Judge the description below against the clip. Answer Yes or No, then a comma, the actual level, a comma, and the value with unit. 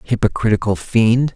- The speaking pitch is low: Yes, low, 110 Hz